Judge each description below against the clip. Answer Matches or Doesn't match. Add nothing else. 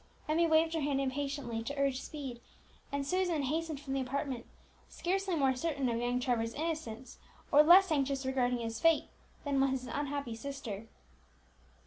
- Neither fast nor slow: Matches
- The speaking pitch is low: Doesn't match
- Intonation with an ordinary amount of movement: Matches